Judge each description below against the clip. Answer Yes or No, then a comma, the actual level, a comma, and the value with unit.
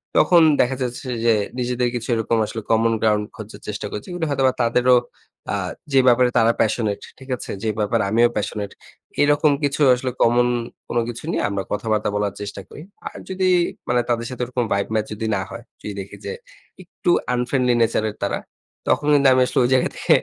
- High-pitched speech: No, low, 120 Hz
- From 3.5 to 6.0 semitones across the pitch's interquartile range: No, average, 3.0 semitones